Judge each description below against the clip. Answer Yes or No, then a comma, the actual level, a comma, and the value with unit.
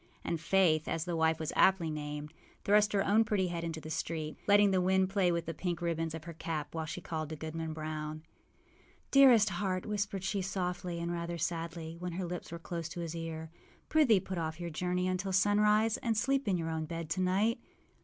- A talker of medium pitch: Yes, medium, 175 Hz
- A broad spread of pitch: No, average, 3.1 semitones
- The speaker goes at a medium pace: No, fast, 215 wpm